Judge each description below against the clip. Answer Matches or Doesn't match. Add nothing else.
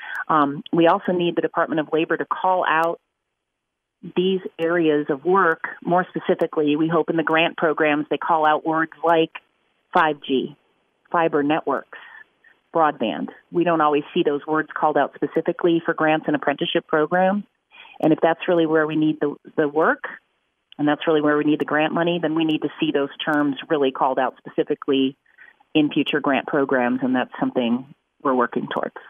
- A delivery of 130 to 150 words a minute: Doesn't match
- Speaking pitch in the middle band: Matches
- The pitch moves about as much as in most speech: Doesn't match